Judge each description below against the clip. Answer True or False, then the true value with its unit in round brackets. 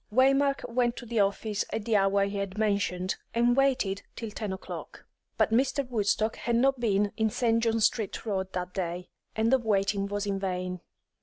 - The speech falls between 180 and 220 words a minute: True (185 wpm)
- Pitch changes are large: False (3.2 semitones)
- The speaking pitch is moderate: False (210 Hz)